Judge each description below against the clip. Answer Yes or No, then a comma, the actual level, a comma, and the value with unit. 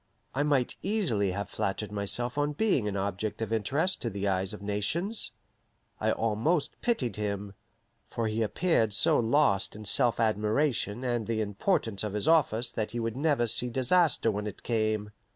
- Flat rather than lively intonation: No, average, 4.8 semitones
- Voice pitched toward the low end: Yes, low, 115 Hz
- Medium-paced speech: Yes, average, 170 wpm